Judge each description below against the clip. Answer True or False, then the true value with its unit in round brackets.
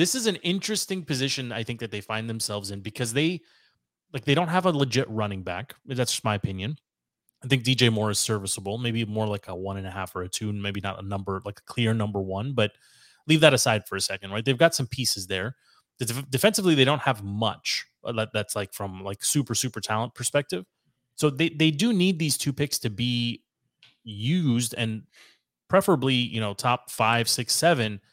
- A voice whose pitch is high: False (115 Hz)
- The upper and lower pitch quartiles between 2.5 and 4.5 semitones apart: False (5.3 semitones)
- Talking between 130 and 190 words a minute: False (205 wpm)